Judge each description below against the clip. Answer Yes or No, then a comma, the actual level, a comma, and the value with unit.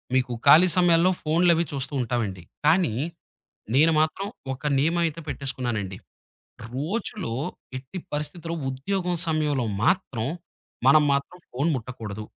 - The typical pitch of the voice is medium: Yes, medium, 150 Hz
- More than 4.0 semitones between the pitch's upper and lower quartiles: Yes, average, 5.0 semitones